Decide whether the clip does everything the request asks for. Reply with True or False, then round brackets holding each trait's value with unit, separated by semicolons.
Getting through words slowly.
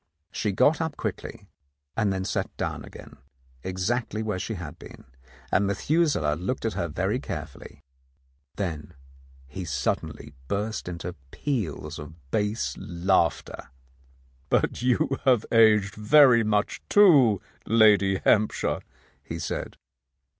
True (125 wpm)